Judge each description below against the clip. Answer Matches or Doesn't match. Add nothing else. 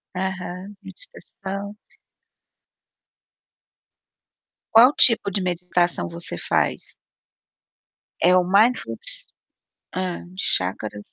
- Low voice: Doesn't match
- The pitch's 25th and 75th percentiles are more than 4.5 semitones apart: Doesn't match